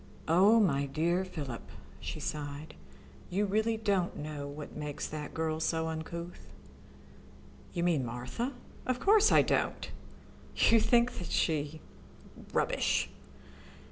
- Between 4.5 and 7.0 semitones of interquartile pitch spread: Yes, wide, 5.4 semitones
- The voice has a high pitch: No, medium, 160 Hz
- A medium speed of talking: No, slow, 120 wpm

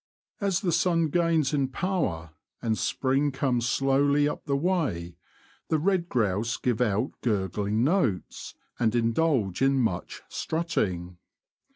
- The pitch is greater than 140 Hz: No, low, 135 Hz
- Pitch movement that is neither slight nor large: No, wide, 7.0 semitones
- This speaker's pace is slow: Yes, slow, 130 wpm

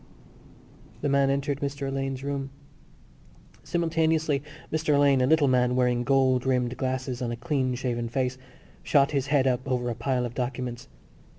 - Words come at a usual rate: Yes, average, 160 wpm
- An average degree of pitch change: No, narrow, 2.0 semitones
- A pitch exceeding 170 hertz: No, low, 130 Hz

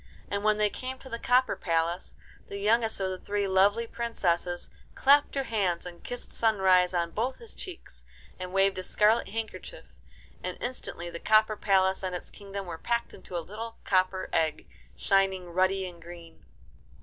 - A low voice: No, high, 195 Hz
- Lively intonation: No, average, 3.8 semitones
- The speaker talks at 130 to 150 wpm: No, average, 175 wpm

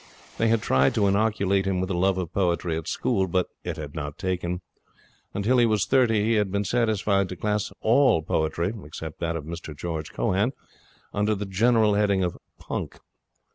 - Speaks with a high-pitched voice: No, very low, 95 Hz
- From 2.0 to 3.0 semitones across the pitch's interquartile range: No, average, 3.8 semitones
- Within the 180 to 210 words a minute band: Yes, average, 185 wpm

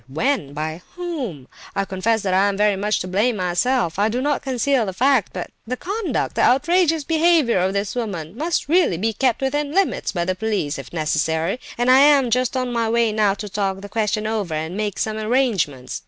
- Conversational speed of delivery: No, fast, 210 wpm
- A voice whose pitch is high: Yes, high, 220 Hz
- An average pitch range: No, wide, 5.8 semitones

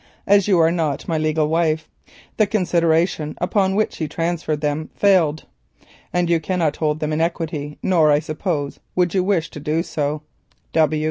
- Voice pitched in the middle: Yes, medium, 160 Hz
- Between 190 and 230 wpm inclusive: No, average, 165 wpm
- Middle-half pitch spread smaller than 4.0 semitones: Yes, narrow, 2.6 semitones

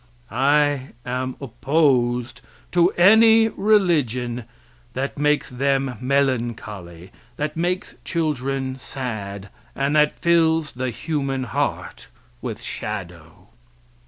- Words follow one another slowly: Yes, slow, 95 wpm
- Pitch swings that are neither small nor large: Yes, average, 3.9 semitones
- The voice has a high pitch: No, low, 135 Hz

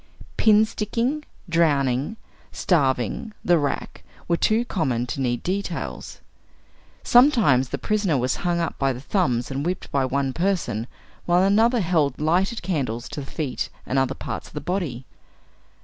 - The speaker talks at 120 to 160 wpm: Yes, average, 150 wpm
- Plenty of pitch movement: Yes, wide, 6.7 semitones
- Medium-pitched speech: Yes, medium, 160 Hz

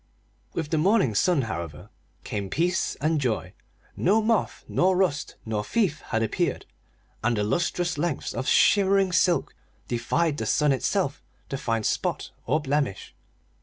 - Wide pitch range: Yes, wide, 7.8 semitones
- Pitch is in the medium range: Yes, medium, 150 Hz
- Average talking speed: Yes, average, 145 wpm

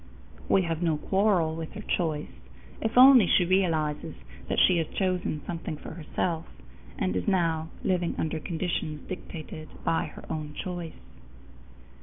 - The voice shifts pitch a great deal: No, average, 2.8 semitones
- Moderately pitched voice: Yes, medium, 165 Hz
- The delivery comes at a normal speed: Yes, average, 145 wpm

